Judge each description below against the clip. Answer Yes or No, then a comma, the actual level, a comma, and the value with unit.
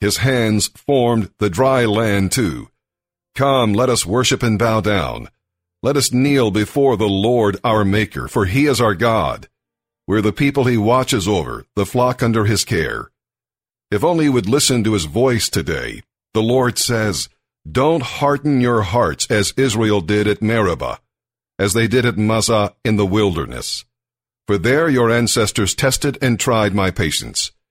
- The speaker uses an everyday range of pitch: Yes, average, 3.4 semitones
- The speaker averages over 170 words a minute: No, average, 165 wpm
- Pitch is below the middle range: Yes, low, 115 Hz